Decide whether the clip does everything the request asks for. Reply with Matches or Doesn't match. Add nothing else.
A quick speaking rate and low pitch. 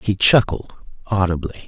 Doesn't match